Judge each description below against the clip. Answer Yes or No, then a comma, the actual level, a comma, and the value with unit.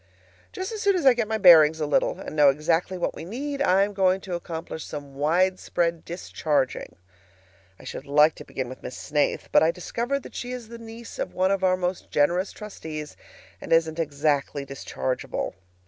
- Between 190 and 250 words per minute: Yes, average, 195 wpm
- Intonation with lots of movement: Yes, wide, 5.7 semitones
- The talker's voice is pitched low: No, medium, 175 Hz